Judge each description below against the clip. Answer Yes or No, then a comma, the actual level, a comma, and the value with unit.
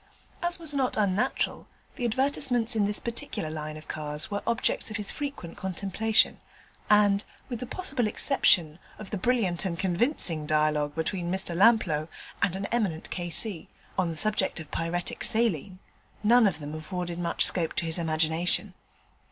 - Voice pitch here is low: No, high, 190 Hz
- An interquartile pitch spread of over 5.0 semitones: Yes, wide, 5.5 semitones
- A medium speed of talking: Yes, average, 160 wpm